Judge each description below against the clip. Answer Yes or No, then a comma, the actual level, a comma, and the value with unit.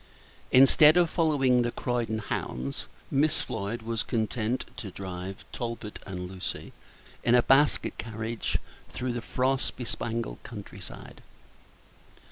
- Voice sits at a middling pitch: No, low, 115 Hz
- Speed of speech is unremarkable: No, slow, 120 wpm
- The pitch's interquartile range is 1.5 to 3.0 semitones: No, average, 3.5 semitones